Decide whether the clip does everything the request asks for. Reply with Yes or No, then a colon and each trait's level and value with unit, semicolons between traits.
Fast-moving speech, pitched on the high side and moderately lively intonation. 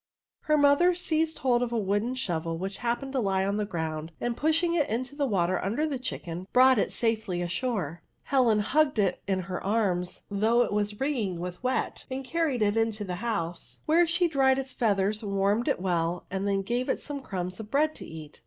No: fast, 210 wpm; high, 220 Hz; wide, 5.8 semitones